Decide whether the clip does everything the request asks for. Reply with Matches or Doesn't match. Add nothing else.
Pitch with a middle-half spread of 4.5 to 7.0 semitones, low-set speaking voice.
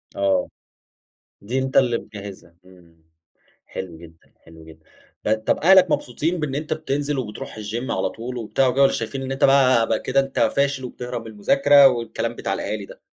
Matches